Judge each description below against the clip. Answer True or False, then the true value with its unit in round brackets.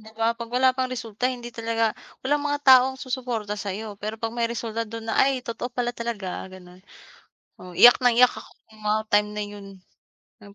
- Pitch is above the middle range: True (230 Hz)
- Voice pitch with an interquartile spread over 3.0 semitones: False (2.7 semitones)